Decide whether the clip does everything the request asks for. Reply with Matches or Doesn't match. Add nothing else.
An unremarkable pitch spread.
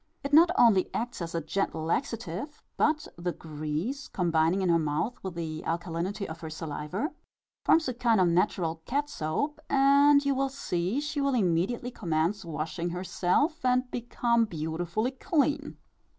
Doesn't match